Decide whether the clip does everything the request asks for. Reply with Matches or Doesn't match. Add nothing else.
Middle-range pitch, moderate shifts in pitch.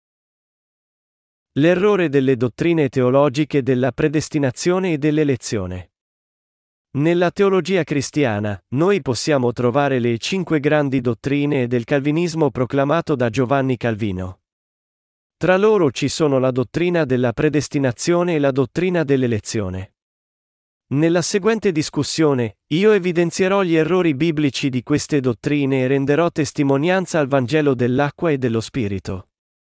Matches